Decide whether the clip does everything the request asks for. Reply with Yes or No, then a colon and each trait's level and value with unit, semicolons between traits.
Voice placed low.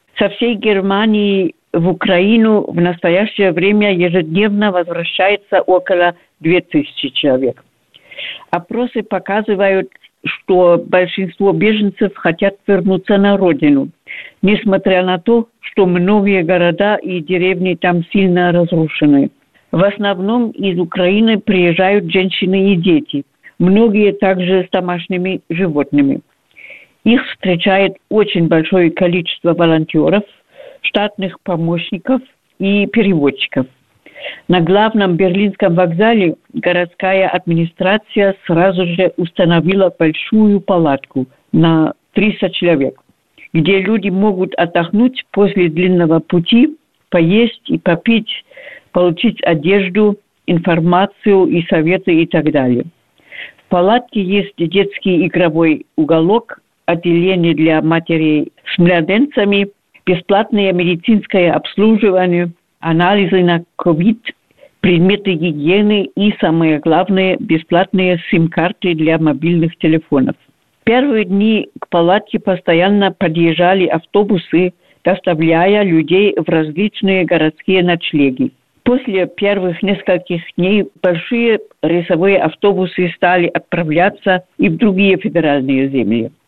No: medium, 185 Hz